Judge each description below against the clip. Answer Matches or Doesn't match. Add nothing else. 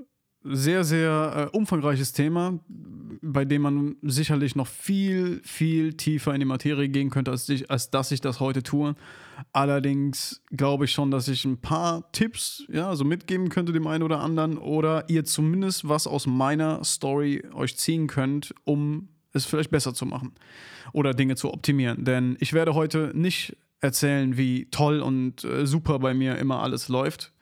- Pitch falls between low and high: Matches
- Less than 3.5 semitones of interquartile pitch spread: Matches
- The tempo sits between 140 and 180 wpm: Matches